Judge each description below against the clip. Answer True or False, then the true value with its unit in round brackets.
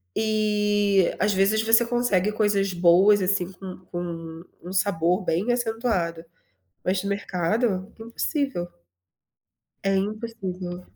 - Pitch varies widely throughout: False (3.2 semitones)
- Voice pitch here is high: True (195 Hz)